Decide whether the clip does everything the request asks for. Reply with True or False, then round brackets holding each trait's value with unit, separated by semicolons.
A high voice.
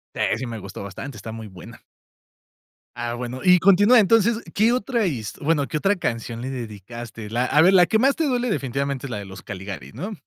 False (130 Hz)